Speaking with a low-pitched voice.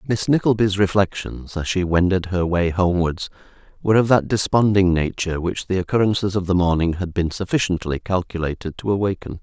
Yes: very low, 95 Hz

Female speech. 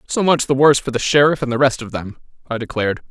No: male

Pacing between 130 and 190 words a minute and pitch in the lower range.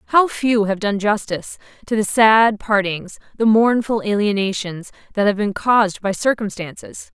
No: average, 150 wpm; high, 210 Hz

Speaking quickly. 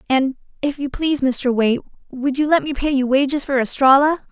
Yes: fast, 210 wpm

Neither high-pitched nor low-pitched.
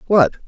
Yes: medium, 165 Hz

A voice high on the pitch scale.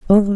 Yes: high, 200 Hz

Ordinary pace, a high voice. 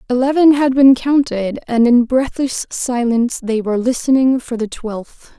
Yes: average, 155 wpm; very high, 250 Hz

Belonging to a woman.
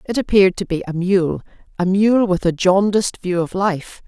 Yes: female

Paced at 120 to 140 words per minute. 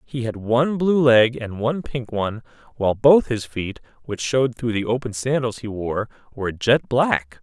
No: average, 180 wpm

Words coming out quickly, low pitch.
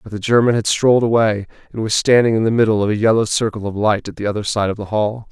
Yes: fast, 280 wpm; low, 110 Hz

